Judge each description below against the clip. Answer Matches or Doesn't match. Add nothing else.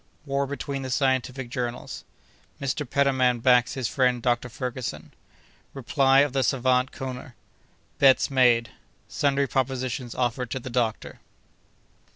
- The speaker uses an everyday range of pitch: Doesn't match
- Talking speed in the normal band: Doesn't match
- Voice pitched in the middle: Doesn't match